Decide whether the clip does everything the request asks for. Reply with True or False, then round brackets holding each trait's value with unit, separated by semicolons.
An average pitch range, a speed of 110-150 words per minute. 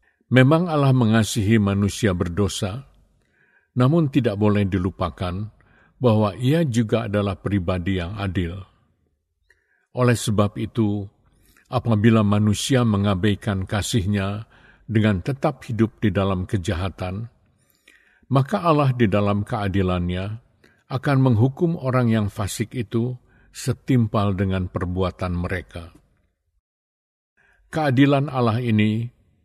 False (4.1 semitones; 95 wpm)